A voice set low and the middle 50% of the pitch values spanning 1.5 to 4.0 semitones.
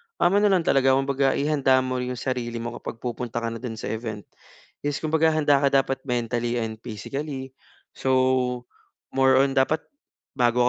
Yes: low, 130 Hz; narrow, 2.5 semitones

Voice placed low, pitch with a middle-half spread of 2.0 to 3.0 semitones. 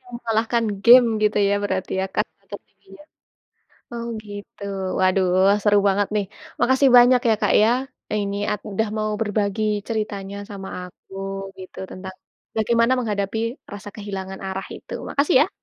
No: high, 210 Hz; average, 2.7 semitones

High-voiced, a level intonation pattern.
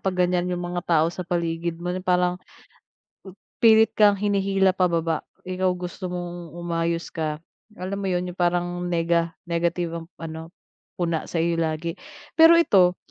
No: medium, 175 Hz; narrow, 1.5 semitones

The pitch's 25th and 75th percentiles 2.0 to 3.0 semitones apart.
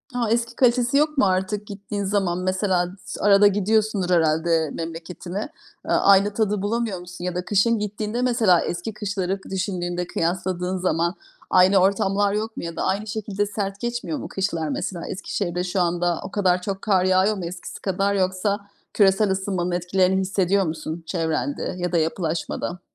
Yes: narrow, 2.6 semitones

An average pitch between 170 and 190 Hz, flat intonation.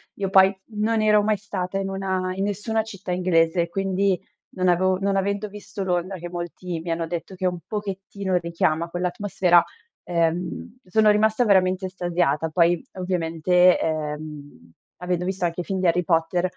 Yes: medium, 185 Hz; narrow, 2.3 semitones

